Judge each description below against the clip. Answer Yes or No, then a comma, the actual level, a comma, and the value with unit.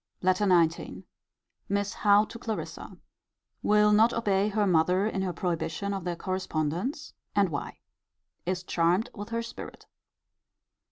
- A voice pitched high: Yes, high, 195 Hz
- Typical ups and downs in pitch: Yes, average, 3.0 semitones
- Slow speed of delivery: Yes, slow, 130 wpm